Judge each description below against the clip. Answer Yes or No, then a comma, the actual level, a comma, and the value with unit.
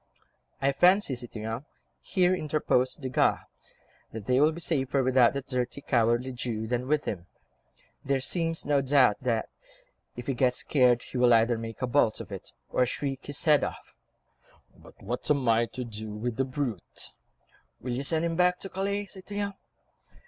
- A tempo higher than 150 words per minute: Yes, average, 170 wpm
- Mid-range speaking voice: No, low, 130 Hz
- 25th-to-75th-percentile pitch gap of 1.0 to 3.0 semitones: No, average, 3.9 semitones